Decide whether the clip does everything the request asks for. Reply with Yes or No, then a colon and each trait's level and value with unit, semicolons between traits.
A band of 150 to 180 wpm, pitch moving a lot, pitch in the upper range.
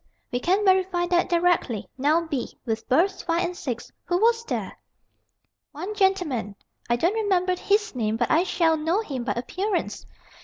Yes: average, 165 wpm; wide, 6.6 semitones; very high, 345 Hz